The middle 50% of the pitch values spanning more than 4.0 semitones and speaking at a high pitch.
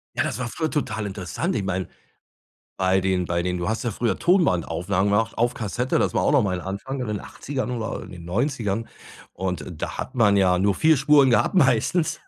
No: wide, 5.6 semitones; low, 105 Hz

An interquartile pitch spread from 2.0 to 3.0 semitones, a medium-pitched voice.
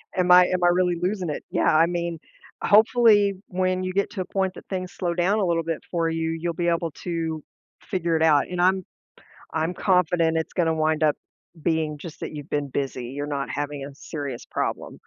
Yes: average, 2.7 semitones; medium, 170 Hz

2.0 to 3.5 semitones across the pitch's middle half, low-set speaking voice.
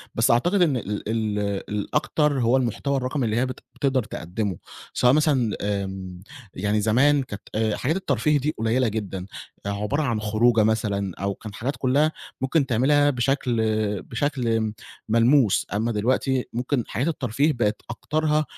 No: average, 4.5 semitones; low, 120 Hz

